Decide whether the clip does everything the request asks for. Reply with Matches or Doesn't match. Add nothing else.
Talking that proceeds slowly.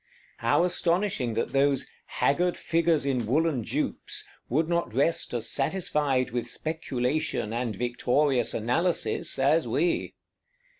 Matches